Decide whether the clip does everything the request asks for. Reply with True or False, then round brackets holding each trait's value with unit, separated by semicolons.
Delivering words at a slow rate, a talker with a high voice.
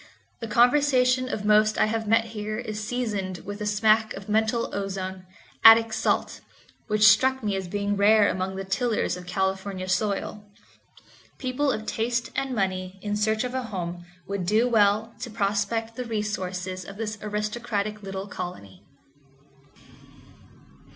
False (150 wpm; 210 Hz)